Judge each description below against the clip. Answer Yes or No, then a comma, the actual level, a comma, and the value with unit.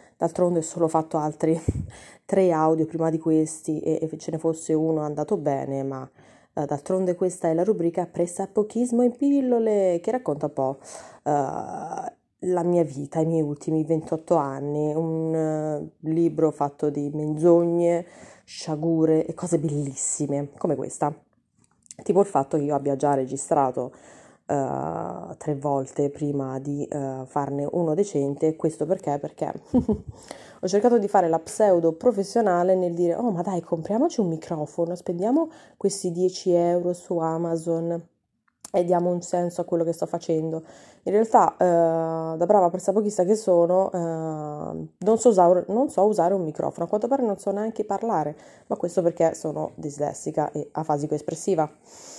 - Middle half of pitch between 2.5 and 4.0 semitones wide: Yes, average, 3.4 semitones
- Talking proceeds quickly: No, average, 160 wpm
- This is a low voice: No, medium, 165 Hz